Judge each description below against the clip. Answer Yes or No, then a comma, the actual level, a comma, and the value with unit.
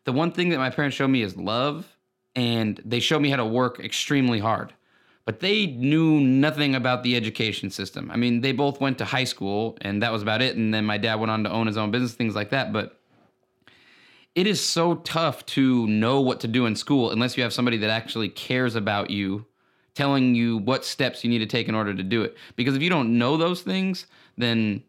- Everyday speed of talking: No, fast, 230 wpm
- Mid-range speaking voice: No, low, 125 Hz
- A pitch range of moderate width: Yes, average, 3.7 semitones